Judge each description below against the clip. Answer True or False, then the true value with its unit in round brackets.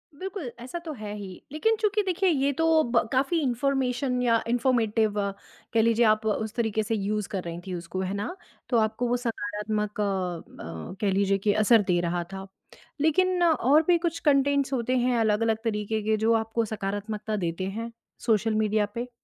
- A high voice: True (225 Hz)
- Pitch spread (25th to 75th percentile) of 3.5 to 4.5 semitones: True (4.2 semitones)